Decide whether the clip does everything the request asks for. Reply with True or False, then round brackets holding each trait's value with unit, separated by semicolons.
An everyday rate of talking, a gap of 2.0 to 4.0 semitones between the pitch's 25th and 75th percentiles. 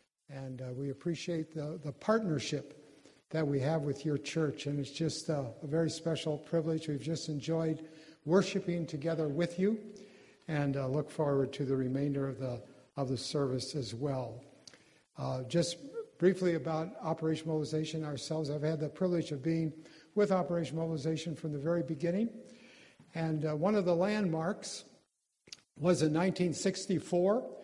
True (155 wpm; 2.9 semitones)